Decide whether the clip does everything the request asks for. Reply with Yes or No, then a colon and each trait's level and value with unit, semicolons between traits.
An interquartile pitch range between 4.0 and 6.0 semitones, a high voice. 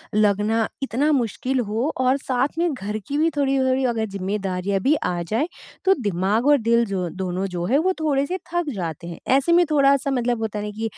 Yes: wide, 5.5 semitones; high, 235 Hz